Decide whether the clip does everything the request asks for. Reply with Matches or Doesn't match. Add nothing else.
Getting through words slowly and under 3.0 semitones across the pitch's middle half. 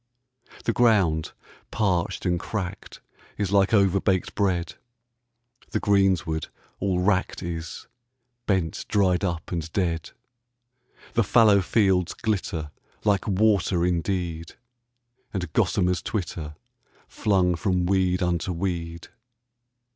Matches